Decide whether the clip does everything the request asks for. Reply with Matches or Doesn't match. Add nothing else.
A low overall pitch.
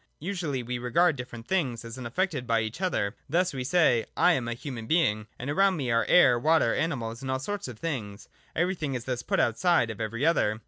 Matches